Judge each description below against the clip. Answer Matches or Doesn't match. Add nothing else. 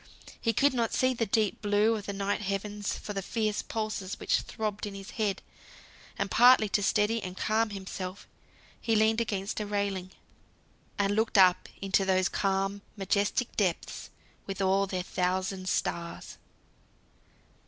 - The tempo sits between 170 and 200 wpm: Doesn't match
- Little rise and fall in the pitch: Matches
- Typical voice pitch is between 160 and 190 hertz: Doesn't match